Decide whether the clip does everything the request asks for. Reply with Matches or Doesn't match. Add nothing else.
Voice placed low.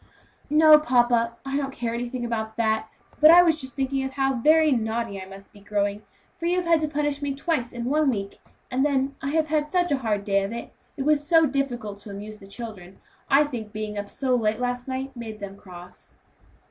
Doesn't match